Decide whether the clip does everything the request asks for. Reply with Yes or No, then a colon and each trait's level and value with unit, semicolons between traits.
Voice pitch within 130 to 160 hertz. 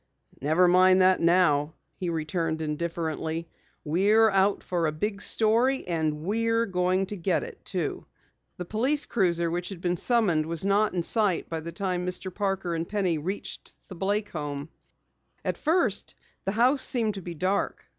No: medium, 185 Hz